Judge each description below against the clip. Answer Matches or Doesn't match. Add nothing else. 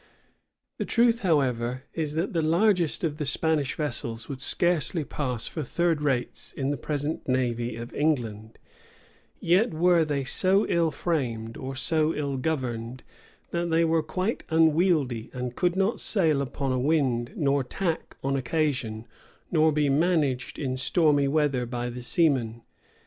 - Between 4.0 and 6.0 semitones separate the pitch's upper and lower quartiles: Matches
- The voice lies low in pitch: Doesn't match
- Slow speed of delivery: Doesn't match